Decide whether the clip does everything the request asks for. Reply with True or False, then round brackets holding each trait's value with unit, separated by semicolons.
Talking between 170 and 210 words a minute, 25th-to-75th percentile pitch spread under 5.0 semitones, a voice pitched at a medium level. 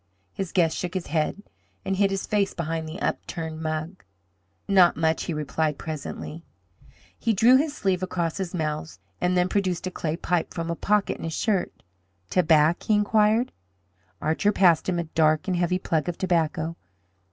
True (175 wpm; 3.2 semitones; 175 Hz)